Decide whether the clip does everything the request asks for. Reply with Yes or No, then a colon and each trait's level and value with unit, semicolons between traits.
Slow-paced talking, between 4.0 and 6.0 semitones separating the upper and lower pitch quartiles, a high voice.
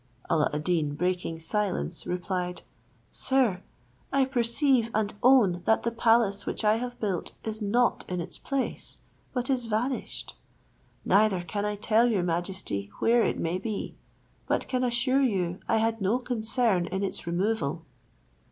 No: average, 150 wpm; average, 4.9 semitones; high, 210 Hz